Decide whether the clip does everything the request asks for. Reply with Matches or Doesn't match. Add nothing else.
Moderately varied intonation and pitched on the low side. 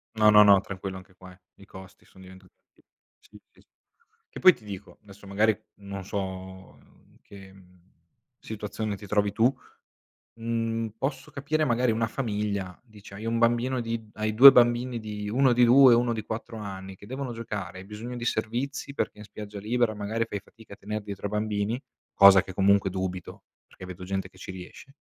Matches